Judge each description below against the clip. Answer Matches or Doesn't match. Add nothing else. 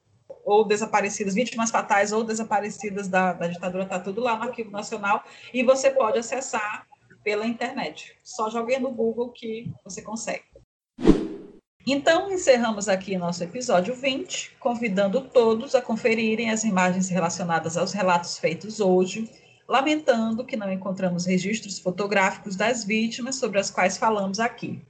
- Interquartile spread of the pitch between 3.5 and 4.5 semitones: Matches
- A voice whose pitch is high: Matches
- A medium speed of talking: Matches